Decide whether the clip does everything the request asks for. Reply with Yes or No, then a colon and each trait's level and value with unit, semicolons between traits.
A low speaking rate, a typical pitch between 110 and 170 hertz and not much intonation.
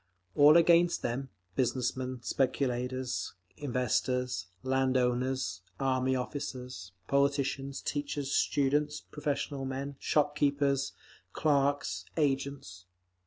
Yes: slow, 90 wpm; low, 135 Hz; narrow, 1.9 semitones